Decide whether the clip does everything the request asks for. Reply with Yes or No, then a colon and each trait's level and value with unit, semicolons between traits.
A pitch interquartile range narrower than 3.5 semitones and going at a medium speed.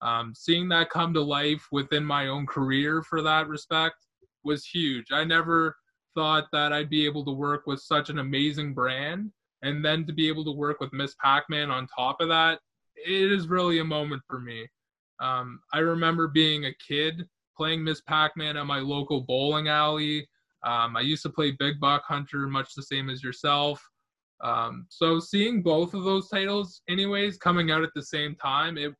Yes: narrow, 2.4 semitones; average, 195 wpm